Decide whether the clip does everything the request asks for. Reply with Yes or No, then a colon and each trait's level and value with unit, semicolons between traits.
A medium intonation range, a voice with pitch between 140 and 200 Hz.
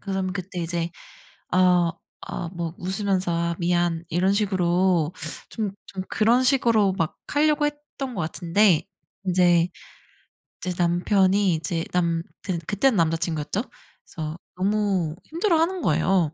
Yes: average, 3.4 semitones; medium, 185 Hz